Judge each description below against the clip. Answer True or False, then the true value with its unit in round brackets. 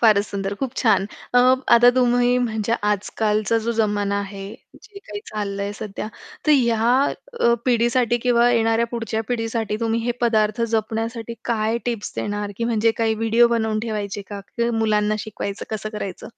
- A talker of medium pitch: False (225 Hz)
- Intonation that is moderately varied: False (2.0 semitones)